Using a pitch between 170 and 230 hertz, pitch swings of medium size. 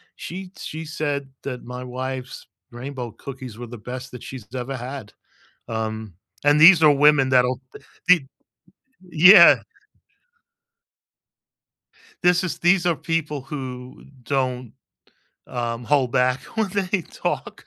No: low, 135 Hz; average, 3.8 semitones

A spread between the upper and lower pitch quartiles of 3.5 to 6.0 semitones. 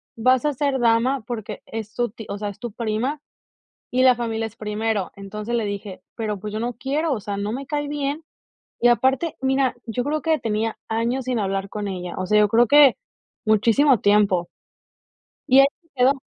Yes: average, 4.0 semitones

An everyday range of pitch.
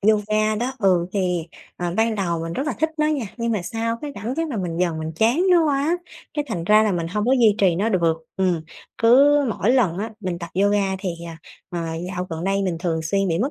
Yes: average, 4.9 semitones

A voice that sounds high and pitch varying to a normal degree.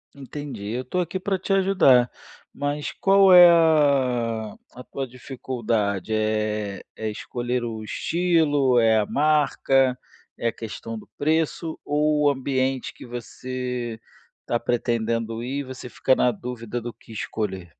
No: low, 125 Hz; average, 4.3 semitones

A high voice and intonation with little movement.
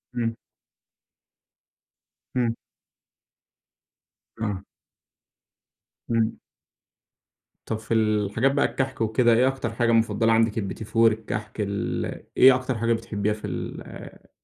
No: low, 115 Hz; narrow, 1.6 semitones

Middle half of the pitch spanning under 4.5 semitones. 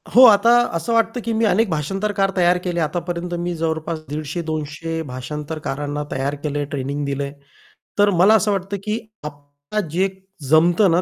No: average, 4.8 semitones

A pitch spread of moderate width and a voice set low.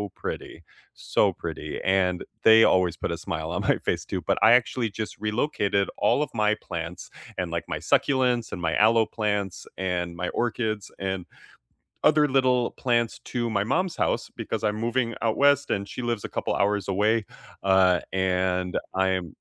Yes: average, 4.2 semitones; low, 105 Hz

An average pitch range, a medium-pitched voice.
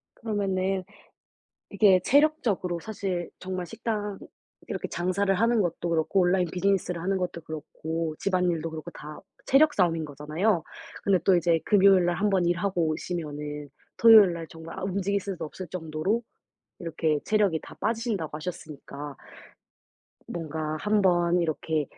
Yes: average, 3.6 semitones; medium, 180 Hz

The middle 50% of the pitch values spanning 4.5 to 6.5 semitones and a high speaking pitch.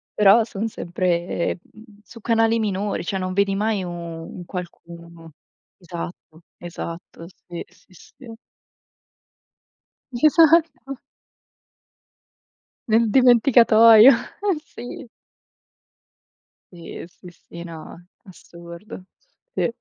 Yes: average, 4.9 semitones; high, 195 Hz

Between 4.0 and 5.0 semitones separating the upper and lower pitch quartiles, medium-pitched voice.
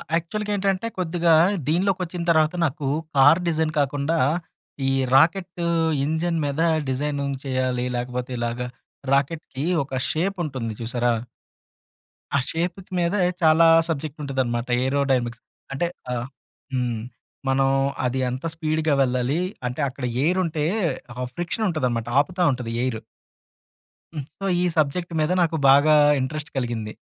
Yes: average, 4.5 semitones; medium, 145 Hz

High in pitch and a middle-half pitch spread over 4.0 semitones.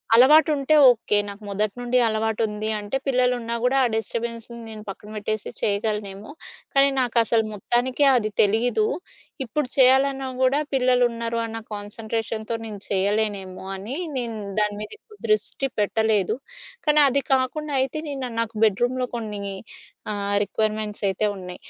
No: high, 225 Hz; average, 3.2 semitones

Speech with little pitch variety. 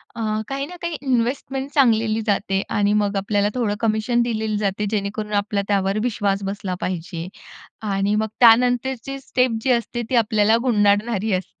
No: average, 3.0 semitones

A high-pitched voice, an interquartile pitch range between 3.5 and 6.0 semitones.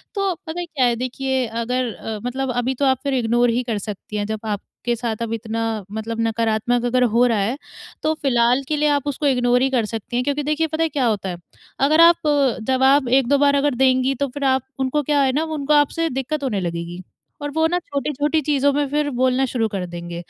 Yes: very high, 260 Hz; average, 3.8 semitones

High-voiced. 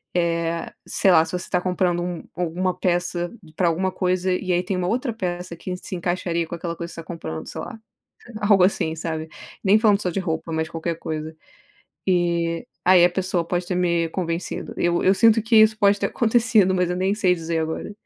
No: medium, 180 Hz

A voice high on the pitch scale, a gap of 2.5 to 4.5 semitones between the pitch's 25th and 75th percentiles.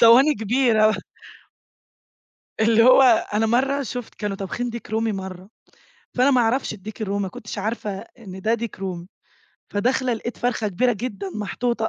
Yes: high, 225 Hz; average, 3.2 semitones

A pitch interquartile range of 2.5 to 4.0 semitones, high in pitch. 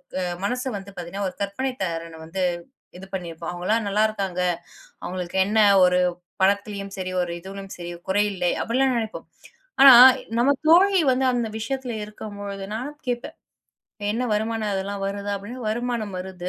Yes: average, 3.6 semitones; high, 200 Hz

